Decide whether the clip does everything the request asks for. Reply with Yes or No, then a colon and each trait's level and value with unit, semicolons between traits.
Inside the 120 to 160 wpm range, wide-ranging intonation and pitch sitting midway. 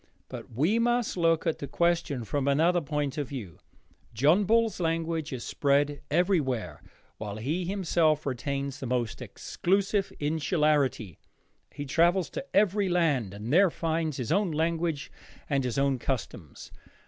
No: average, 145 wpm; average, 4.3 semitones; medium, 155 Hz